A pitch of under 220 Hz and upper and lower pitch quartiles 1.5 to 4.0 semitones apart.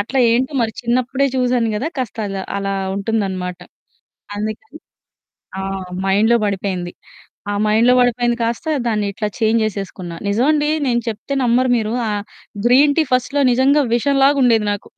No: high, 230 Hz; average, 3.7 semitones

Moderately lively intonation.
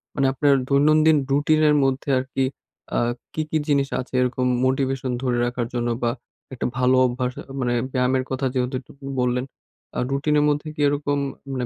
No: narrow, 2.2 semitones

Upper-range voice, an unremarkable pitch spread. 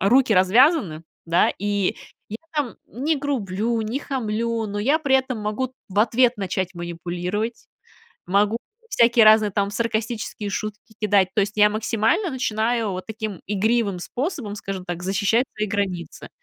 Yes: high, 215 Hz; average, 3.1 semitones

